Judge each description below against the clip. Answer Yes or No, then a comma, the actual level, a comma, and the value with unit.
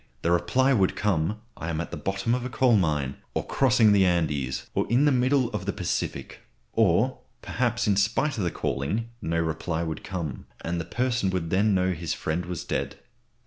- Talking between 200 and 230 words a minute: Yes, fast, 205 wpm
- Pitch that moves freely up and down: Yes, wide, 6.0 semitones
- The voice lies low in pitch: Yes, very low, 95 Hz